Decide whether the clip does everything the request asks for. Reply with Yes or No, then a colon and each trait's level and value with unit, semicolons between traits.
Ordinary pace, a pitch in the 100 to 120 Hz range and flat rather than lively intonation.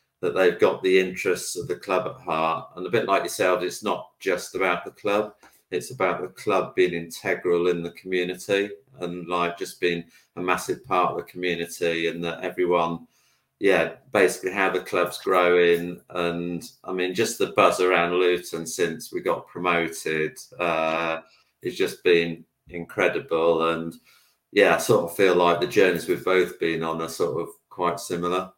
No: average, 180 wpm; very low, 90 Hz; narrow, 1.4 semitones